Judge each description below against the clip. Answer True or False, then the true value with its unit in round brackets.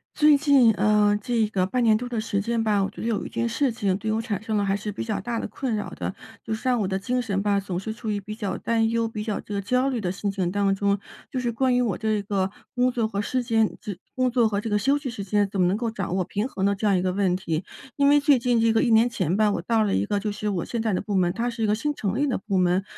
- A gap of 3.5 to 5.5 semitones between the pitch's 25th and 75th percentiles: False (2.8 semitones)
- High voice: True (215 Hz)